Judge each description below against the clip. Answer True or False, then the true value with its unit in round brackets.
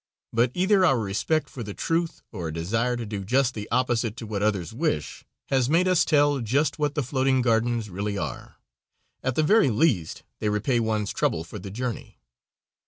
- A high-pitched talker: False (120 Hz)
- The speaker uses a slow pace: False (190 wpm)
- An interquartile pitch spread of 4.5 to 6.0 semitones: True (5.2 semitones)